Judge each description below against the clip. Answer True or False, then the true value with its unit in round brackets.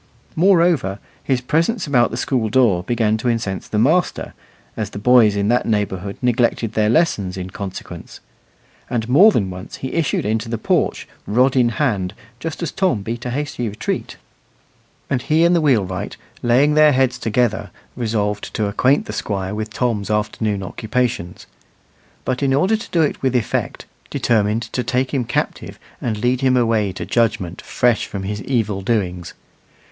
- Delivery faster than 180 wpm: False (170 wpm)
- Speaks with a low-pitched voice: True (115 Hz)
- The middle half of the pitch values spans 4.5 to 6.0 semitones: False (4.0 semitones)